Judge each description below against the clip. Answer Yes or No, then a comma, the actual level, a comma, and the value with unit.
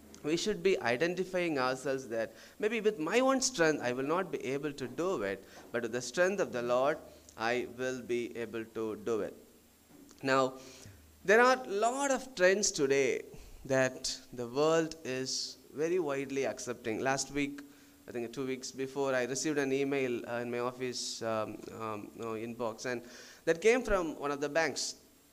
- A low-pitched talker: Yes, low, 130 Hz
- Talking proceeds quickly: Yes, fast, 175 wpm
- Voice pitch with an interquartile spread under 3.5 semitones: No, average, 5.2 semitones